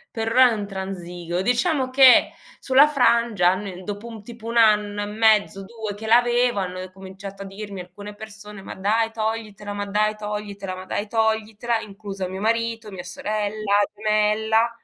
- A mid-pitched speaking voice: No, high, 210 Hz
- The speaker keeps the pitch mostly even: Yes, narrow, 2.2 semitones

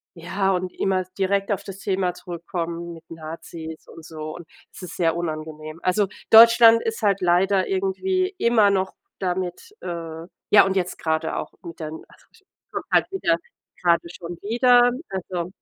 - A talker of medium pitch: Yes, medium, 180 Hz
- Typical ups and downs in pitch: Yes, average, 3.1 semitones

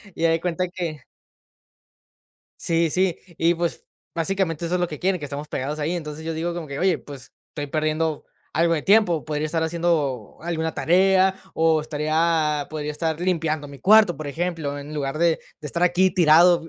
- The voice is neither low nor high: Yes, medium, 165 Hz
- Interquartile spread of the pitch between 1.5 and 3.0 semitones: Yes, narrow, 2.4 semitones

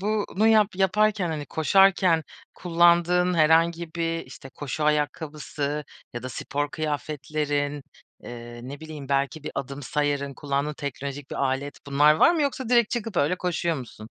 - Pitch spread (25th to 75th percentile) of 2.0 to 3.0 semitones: No, average, 3.9 semitones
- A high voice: No, medium, 155 Hz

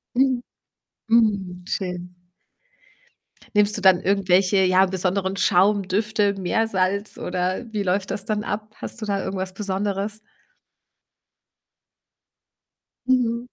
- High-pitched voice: Yes, high, 200 Hz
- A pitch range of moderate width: No, narrow, 2.3 semitones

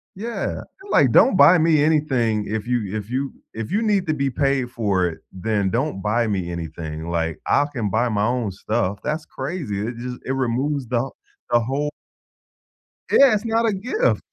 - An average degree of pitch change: No, wide, 6.3 semitones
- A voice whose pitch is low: Yes, low, 125 Hz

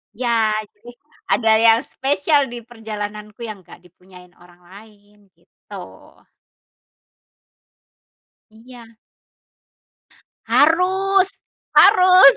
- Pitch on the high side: Yes, high, 225 Hz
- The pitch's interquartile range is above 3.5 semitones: Yes, average, 5.1 semitones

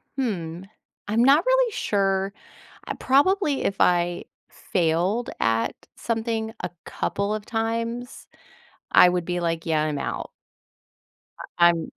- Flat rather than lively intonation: No, wide, 5.4 semitones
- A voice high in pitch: Yes, high, 200 Hz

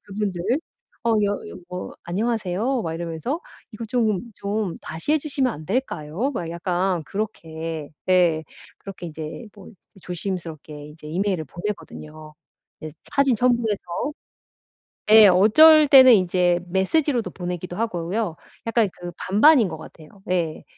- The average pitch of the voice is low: No, high, 190 Hz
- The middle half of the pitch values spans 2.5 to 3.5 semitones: No, wide, 5.4 semitones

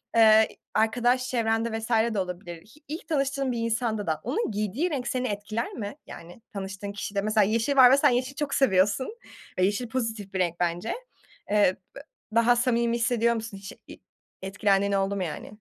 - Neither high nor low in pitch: No, high, 220 Hz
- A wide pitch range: No, average, 3.7 semitones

